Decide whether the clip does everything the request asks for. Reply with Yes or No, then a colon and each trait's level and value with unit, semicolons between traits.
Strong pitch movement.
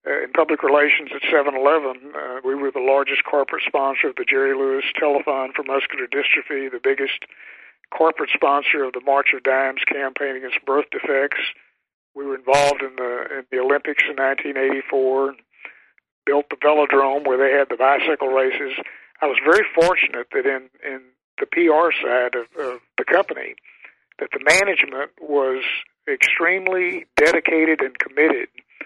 No: average, 3.2 semitones